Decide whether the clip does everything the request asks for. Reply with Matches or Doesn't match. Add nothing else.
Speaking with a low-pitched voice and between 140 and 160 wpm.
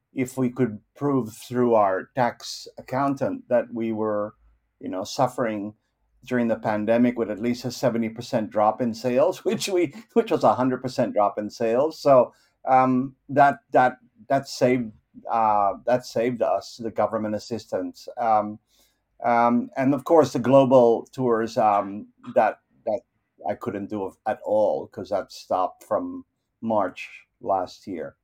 Matches